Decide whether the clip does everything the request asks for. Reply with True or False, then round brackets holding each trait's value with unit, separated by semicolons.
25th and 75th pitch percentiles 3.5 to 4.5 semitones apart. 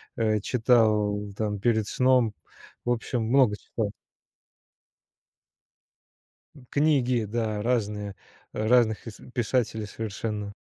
False (2.7 semitones)